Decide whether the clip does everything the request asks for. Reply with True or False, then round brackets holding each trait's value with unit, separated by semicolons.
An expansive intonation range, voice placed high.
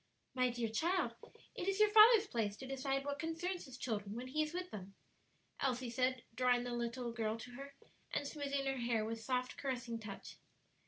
False (3.4 semitones; 255 Hz)